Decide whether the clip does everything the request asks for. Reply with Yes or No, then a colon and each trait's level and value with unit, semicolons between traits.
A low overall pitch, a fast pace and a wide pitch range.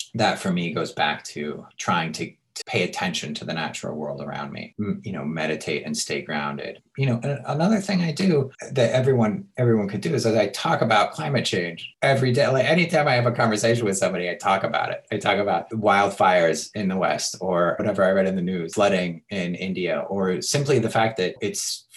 Yes: low, 115 Hz; fast, 215 wpm; wide, 7.3 semitones